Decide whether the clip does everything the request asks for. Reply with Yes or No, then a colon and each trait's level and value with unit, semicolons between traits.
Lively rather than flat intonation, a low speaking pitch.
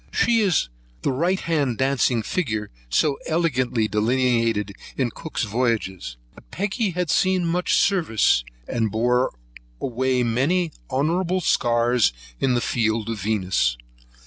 Yes: wide, 6.8 semitones; low, 125 Hz